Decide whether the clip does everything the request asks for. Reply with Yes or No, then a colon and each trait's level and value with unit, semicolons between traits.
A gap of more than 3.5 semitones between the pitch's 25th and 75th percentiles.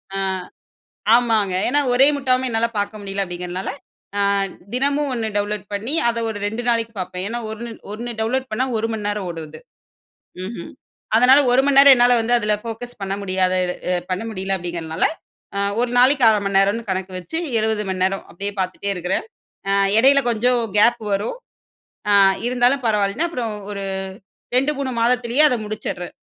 Yes: average, 3.9 semitones